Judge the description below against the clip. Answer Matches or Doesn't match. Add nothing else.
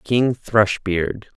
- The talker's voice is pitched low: Matches